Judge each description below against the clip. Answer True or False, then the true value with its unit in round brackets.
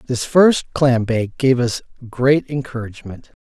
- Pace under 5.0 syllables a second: True (4.3 syllables/s)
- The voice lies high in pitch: False (125 Hz)